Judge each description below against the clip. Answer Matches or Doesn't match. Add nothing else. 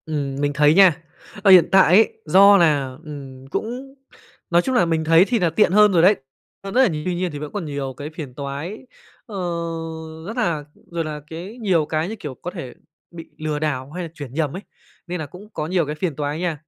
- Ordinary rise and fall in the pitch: Matches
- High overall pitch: Doesn't match